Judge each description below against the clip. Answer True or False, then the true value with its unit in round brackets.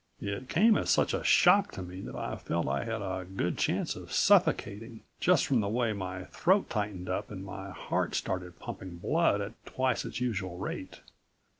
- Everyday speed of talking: True (190 wpm)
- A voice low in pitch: True (100 Hz)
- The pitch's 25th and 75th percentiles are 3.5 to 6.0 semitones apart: True (4.1 semitones)